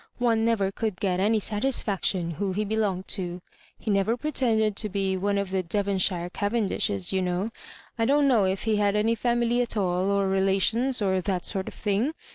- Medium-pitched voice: No, high, 200 Hz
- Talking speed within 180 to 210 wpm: Yes, average, 195 wpm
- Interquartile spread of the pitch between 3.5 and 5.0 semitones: No, average, 3.0 semitones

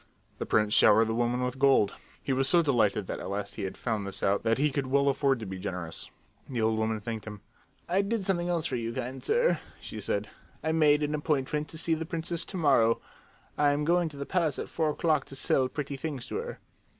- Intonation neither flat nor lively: No, wide, 5.8 semitones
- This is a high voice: No, low, 135 Hz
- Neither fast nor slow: No, fast, 240 wpm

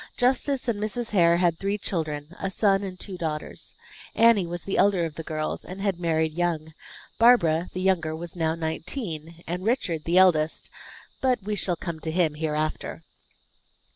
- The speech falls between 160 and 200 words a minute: Yes, average, 170 wpm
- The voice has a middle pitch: Yes, medium, 175 Hz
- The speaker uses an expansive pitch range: No, average, 3.7 semitones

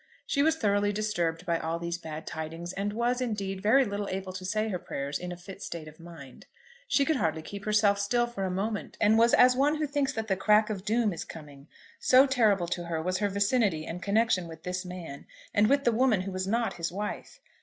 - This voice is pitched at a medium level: No, high, 200 Hz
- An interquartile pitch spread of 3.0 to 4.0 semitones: No, average, 4.5 semitones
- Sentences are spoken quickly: Yes, fast, 230 wpm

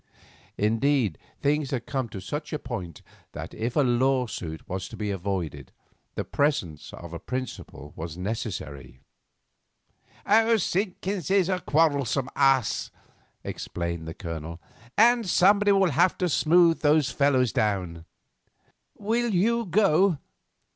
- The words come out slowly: Yes, slow, 125 wpm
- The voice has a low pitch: Yes, low, 130 Hz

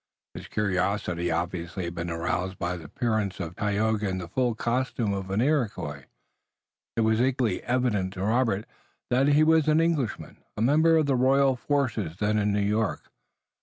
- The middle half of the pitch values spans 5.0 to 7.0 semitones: Yes, wide, 5.6 semitones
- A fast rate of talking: No, average, 170 wpm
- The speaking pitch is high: No, low, 105 Hz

